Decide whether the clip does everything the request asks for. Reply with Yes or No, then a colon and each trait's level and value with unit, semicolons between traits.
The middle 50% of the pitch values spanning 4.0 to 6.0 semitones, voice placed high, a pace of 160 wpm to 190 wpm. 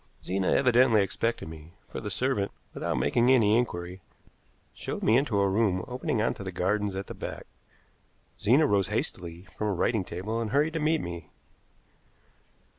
No: average, 4.7 semitones; low, 105 Hz; average, 170 wpm